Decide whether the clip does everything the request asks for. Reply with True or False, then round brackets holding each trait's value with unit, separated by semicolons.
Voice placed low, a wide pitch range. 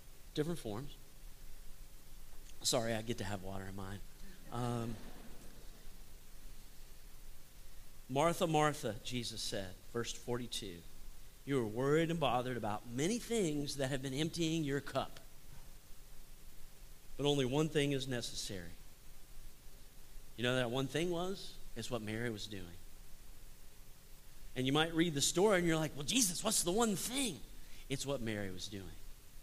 True (125 Hz; 7.0 semitones)